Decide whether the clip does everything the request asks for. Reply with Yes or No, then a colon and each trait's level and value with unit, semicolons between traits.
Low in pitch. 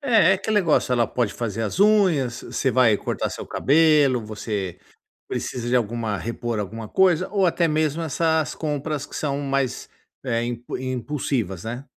Yes: low, 130 Hz